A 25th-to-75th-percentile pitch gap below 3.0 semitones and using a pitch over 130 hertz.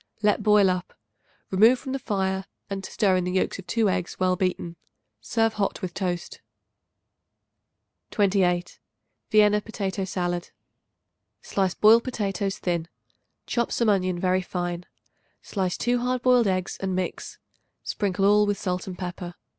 Yes: narrow, 2.4 semitones; high, 190 Hz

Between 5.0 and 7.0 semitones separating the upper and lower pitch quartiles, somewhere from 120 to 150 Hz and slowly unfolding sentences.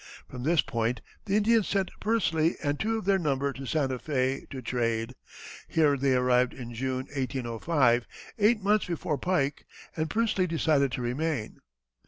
No: wide, 5.6 semitones; medium, 140 Hz; average, 160 wpm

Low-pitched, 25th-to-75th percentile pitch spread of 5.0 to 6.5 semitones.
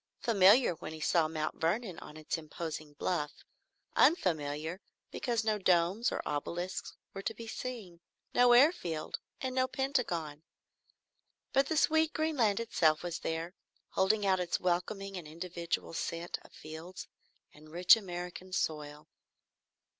No: medium, 180 Hz; wide, 5.6 semitones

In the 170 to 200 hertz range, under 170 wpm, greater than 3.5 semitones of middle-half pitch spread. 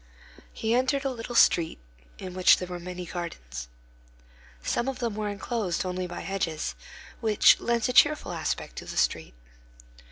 Yes: high, 190 Hz; average, 160 wpm; average, 5.2 semitones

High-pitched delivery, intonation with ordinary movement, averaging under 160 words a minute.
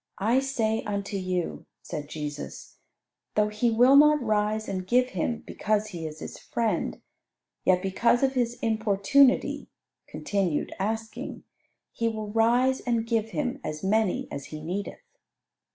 Yes: high, 215 Hz; average, 4.0 semitones; average, 140 wpm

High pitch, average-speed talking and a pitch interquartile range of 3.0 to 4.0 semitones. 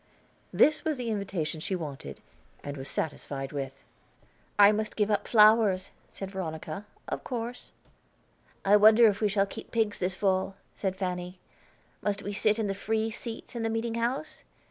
Yes: high, 205 Hz; average, 165 wpm; average, 3.3 semitones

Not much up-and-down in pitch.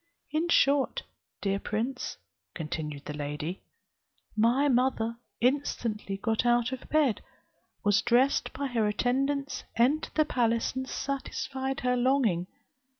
No: average, 4.2 semitones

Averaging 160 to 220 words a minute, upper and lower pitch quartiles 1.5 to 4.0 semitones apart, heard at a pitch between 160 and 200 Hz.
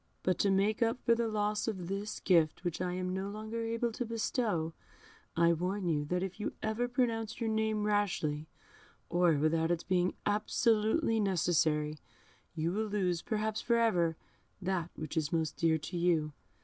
No: average, 175 wpm; average, 4.5 semitones; high, 190 Hz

